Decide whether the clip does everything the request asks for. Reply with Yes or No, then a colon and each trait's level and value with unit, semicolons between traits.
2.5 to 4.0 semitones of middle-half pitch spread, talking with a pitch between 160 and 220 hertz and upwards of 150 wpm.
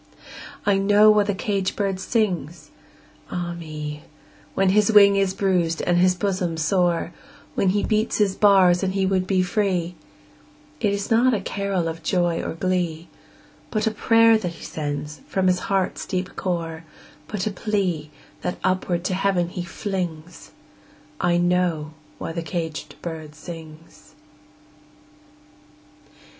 No: average, 2.9 semitones; medium, 185 Hz; average, 145 wpm